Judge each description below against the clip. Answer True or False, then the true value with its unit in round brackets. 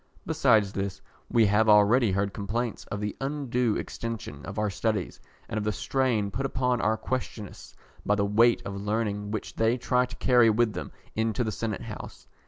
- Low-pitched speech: True (110 Hz)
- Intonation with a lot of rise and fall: False (2.7 semitones)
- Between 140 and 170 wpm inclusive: False (185 wpm)